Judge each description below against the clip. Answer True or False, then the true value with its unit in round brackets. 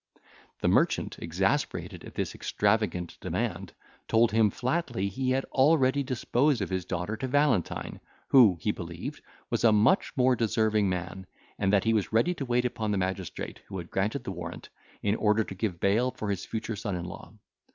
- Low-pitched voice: True (110 Hz)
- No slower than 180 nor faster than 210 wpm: True (185 wpm)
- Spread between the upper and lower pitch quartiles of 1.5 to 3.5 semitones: False (4.6 semitones)